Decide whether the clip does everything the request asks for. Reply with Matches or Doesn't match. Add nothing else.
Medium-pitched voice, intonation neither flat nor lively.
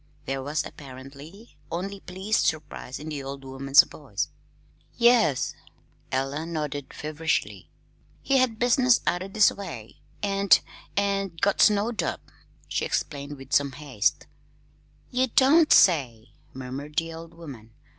Doesn't match